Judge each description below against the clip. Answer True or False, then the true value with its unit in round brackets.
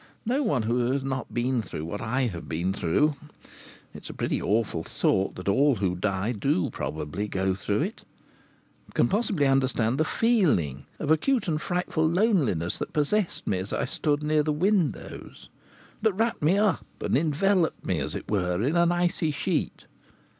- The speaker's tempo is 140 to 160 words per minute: False (175 wpm)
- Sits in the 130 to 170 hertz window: True (140 Hz)